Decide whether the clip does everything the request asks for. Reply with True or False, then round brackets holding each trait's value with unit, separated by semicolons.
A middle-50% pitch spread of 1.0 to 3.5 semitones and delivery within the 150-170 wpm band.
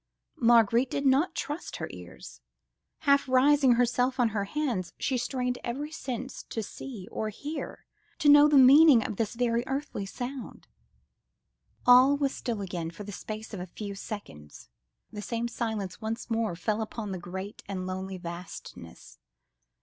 False (4.9 semitones; 155 wpm)